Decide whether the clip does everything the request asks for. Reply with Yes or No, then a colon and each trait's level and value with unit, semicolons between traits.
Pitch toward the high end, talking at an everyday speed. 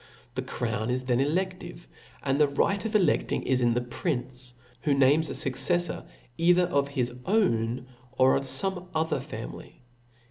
No: medium, 140 Hz; average, 155 wpm